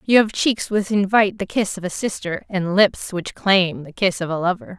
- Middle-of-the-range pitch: No, high, 195 Hz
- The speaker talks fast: Yes, fast, 240 wpm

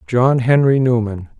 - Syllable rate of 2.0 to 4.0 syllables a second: No, 4.2 syllables/s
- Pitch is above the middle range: No, low, 125 Hz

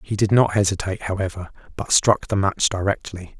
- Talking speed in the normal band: Yes, average, 175 wpm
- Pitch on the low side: Yes, low, 100 Hz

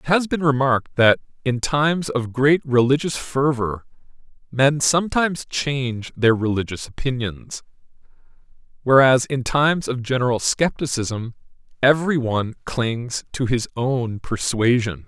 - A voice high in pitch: No, low, 130 Hz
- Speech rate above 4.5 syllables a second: No, 4.4 syllables/s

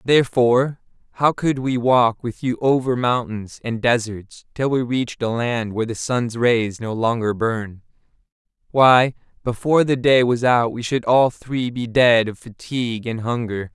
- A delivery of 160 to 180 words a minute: Yes, average, 170 wpm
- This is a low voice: Yes, low, 120 Hz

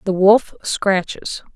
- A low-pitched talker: No, high, 195 Hz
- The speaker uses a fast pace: No, slow, 115 wpm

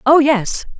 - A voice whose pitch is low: No, very high, 265 Hz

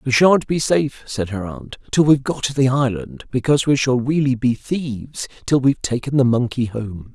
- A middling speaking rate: No, fast, 210 wpm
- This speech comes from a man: Yes, male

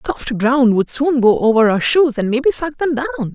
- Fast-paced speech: Yes, fast, 250 wpm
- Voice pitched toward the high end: Yes, very high, 255 Hz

